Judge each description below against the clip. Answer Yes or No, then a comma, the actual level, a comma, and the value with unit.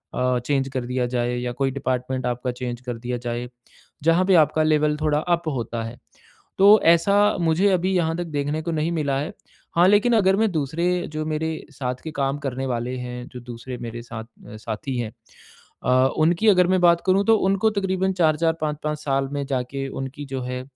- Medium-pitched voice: Yes, medium, 145 Hz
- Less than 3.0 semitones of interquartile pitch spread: No, average, 5.1 semitones